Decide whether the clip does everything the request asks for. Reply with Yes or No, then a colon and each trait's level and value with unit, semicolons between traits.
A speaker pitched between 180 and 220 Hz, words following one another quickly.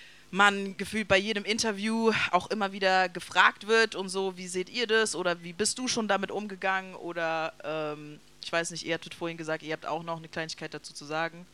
Yes: medium, 185 Hz; fast, 215 wpm